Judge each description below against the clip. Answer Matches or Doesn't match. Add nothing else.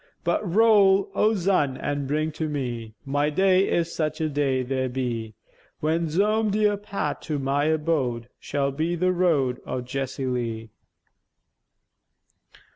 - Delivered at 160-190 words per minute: Doesn't match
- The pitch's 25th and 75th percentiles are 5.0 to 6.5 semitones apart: Matches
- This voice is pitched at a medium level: Matches